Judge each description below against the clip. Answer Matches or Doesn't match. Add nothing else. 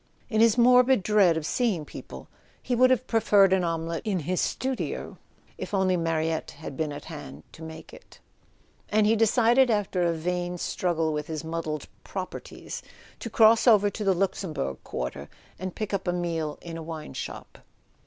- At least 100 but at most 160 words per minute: Doesn't match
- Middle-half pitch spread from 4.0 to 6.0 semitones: Matches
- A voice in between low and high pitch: Matches